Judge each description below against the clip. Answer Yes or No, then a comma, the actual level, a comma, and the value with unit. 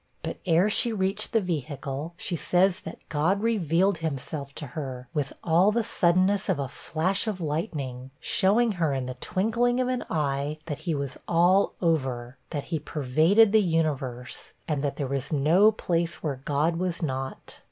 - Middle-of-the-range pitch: Yes, medium, 165 Hz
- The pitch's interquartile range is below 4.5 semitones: No, average, 5.2 semitones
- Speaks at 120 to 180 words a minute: Yes, average, 175 wpm